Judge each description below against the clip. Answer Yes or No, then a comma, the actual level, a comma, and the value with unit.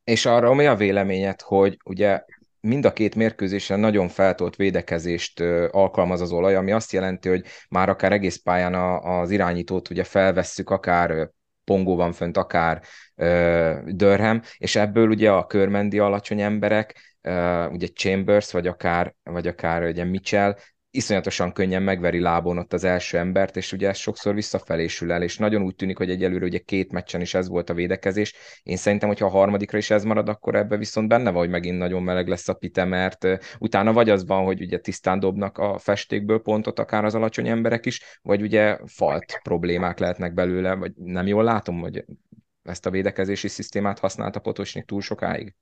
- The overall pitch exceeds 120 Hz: No, very low, 95 Hz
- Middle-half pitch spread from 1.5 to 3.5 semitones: Yes, narrow, 2.4 semitones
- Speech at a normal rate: No, fast, 175 wpm